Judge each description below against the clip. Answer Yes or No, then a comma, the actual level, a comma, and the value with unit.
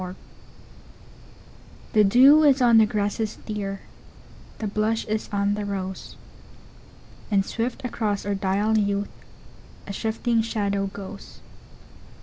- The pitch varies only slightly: Yes, narrow, 2.0 semitones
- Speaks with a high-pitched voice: Yes, high, 210 Hz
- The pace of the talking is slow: Yes, slow, 105 wpm